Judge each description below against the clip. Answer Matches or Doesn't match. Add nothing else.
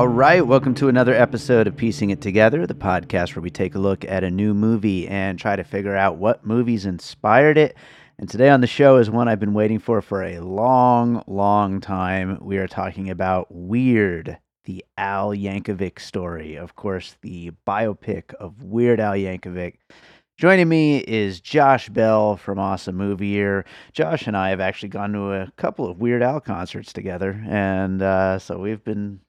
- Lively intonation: Doesn't match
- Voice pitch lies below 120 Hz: Matches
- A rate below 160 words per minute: Doesn't match